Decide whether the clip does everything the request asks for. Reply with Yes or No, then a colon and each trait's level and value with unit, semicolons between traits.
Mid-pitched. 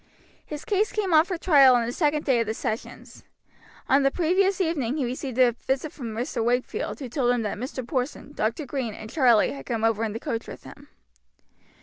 No: very high, 260 Hz